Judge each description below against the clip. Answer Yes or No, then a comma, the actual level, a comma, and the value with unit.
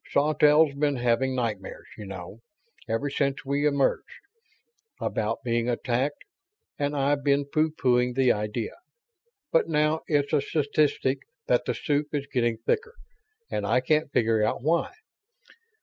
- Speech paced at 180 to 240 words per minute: No, average, 140 wpm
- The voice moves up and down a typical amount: Yes, average, 3.9 semitones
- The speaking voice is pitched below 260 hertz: Yes, medium, 140 Hz